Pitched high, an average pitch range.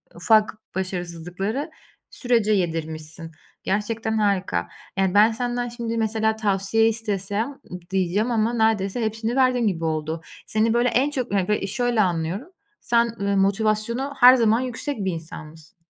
Yes: high, 215 Hz; average, 3.8 semitones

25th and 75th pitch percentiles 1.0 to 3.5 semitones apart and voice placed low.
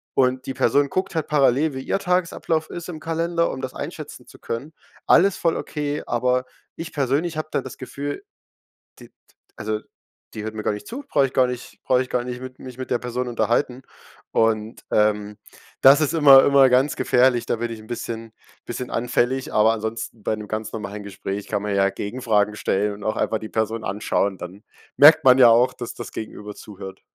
No: average, 4.4 semitones; low, 125 Hz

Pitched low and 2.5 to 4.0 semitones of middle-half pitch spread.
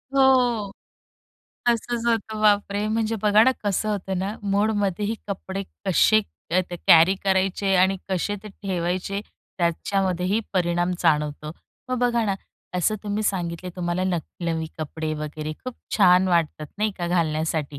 No: high, 190 Hz; average, 3.5 semitones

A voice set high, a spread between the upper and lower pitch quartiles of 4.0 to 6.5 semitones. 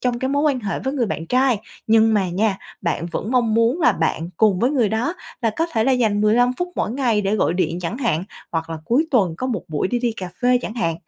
Yes: high, 225 Hz; average, 4.9 semitones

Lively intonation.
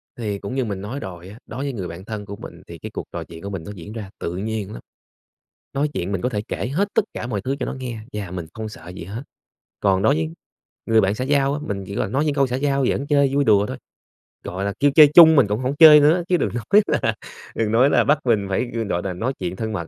Yes: wide, 5.9 semitones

